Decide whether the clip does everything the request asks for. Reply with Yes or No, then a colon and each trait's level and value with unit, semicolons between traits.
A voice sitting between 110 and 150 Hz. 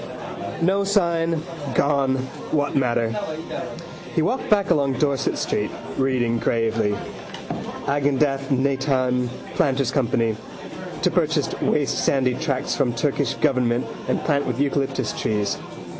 Yes: low, 135 Hz